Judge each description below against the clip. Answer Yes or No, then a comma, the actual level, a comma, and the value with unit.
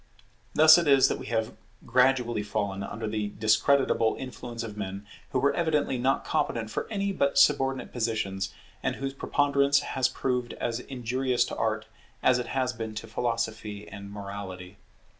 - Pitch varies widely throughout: No, average, 4.0 semitones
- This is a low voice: Yes, low, 120 Hz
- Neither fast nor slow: Yes, average, 160 wpm